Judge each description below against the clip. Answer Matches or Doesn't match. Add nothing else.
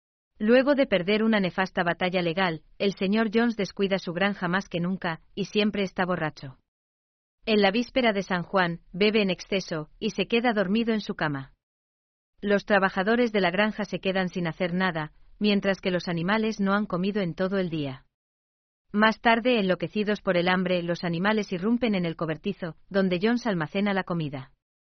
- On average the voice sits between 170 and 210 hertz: Matches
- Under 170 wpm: Doesn't match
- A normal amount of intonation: Matches